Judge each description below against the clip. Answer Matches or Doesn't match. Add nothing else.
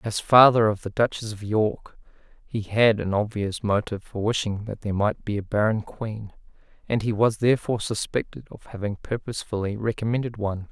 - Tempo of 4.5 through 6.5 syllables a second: Matches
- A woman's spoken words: Doesn't match